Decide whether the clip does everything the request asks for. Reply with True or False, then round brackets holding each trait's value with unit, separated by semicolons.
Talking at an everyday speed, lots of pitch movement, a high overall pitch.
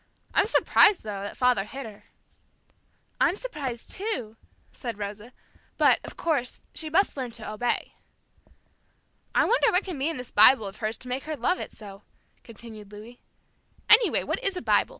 True (175 wpm; 6.9 semitones; 245 Hz)